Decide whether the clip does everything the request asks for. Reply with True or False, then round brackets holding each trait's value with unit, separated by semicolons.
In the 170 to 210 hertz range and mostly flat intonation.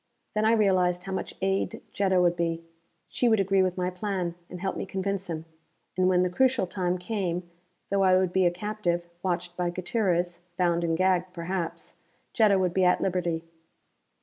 True (185 Hz; 1.7 semitones)